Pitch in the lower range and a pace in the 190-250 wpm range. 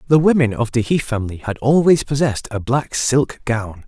Yes: low, 125 Hz; average, 200 wpm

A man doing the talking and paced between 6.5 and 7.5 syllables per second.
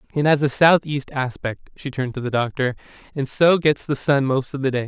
No: male; 5.8 syllables/s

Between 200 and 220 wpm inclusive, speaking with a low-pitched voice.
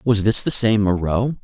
Yes: fast, 210 wpm; low, 110 Hz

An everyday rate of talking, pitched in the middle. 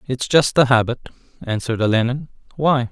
No: average, 145 wpm; low, 125 Hz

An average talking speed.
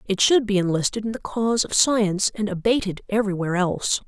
Yes: average, 190 wpm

